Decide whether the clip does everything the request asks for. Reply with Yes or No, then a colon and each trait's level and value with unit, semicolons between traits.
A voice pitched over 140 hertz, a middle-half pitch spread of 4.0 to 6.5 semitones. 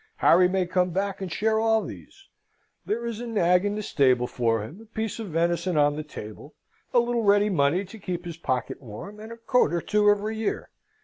Yes: high, 190 Hz; average, 5.0 semitones